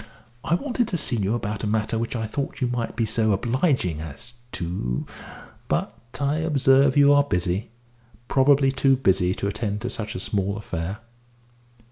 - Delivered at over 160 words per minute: Yes, average, 170 wpm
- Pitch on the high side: No, low, 115 Hz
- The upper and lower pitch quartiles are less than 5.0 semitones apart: No, wide, 5.4 semitones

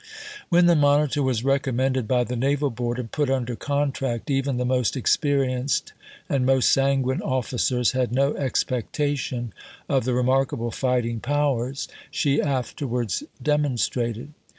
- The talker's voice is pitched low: Yes, low, 130 Hz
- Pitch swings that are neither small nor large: No, narrow, 2.3 semitones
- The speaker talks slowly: Yes, slow, 130 wpm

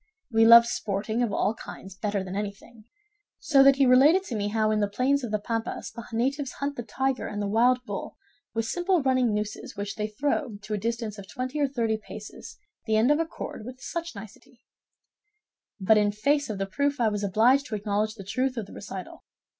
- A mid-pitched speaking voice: No, high, 225 Hz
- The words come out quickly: Yes, fast, 215 wpm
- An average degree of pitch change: Yes, average, 3.8 semitones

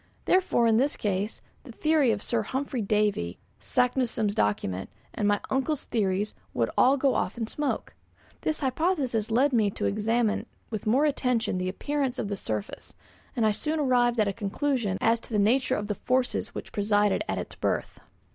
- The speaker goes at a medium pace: Yes, average, 180 wpm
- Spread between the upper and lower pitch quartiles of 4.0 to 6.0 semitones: Yes, average, 4.3 semitones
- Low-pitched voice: No, high, 230 Hz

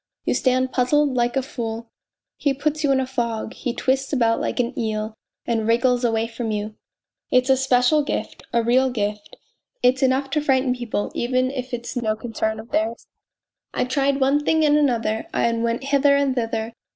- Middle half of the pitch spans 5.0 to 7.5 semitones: No, average, 2.8 semitones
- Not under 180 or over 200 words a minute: Yes, average, 190 wpm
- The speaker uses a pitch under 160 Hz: No, very high, 250 Hz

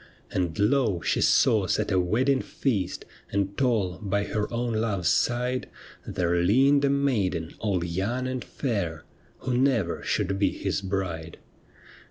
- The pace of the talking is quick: No, average, 145 wpm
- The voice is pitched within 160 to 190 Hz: No, low, 105 Hz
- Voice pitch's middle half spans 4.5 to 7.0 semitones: Yes, average, 5.3 semitones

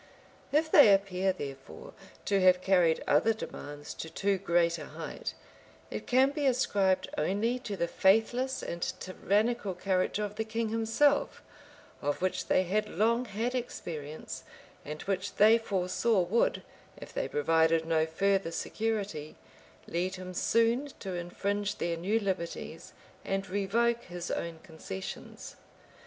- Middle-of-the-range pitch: No, high, 195 Hz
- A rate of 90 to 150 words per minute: Yes, average, 140 wpm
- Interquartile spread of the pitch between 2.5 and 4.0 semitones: No, average, 4.6 semitones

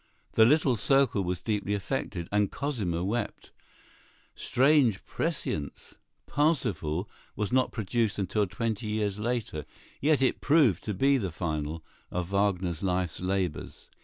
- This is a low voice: Yes, low, 105 Hz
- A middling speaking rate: No, slow, 130 wpm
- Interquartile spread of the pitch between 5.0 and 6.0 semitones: Yes, wide, 5.4 semitones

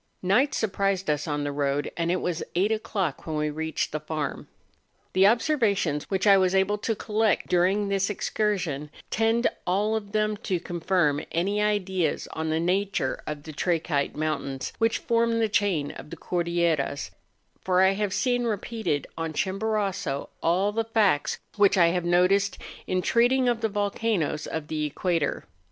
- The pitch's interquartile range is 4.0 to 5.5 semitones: Yes, average, 4.8 semitones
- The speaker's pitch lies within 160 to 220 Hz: Yes, high, 190 Hz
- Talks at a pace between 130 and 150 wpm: No, average, 165 wpm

